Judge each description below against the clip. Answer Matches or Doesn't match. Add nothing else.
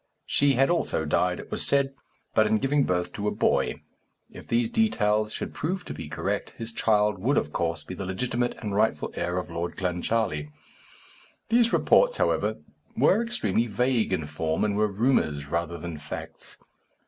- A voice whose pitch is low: Matches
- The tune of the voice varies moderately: Doesn't match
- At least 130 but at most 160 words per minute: Doesn't match